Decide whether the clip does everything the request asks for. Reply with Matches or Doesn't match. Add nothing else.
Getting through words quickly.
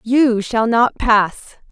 Doesn't match